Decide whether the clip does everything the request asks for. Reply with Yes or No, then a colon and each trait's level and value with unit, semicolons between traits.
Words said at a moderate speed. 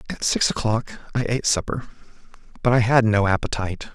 Yes: average, 165 wpm